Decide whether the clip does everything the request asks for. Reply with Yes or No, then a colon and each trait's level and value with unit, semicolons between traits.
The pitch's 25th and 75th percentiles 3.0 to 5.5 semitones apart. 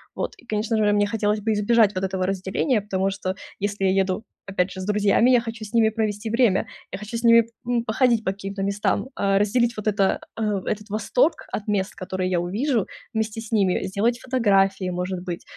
No: narrow, 2.5 semitones